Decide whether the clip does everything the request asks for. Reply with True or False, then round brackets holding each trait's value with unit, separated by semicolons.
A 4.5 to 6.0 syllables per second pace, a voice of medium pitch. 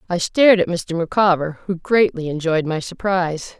True (5.0 syllables/s; 175 Hz)